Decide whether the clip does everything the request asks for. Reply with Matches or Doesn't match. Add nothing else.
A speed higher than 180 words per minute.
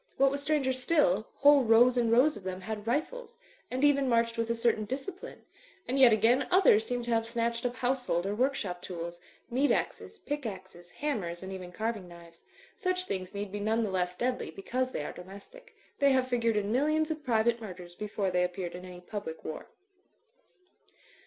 Matches